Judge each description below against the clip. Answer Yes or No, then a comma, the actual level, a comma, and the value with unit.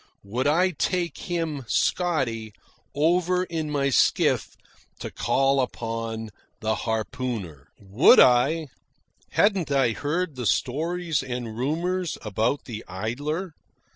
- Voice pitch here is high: No, low, 135 Hz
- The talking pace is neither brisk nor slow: No, slow, 110 wpm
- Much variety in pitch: Yes, wide, 6.5 semitones